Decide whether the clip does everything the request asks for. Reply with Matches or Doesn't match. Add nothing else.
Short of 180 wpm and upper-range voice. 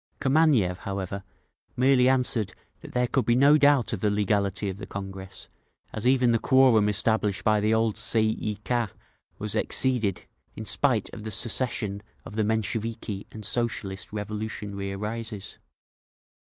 Doesn't match